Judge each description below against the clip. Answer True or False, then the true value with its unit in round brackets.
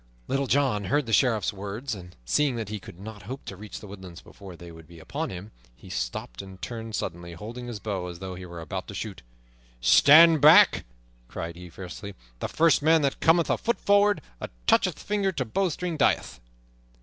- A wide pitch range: True (7.8 semitones)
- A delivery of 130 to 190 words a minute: False (200 wpm)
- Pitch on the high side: False (105 Hz)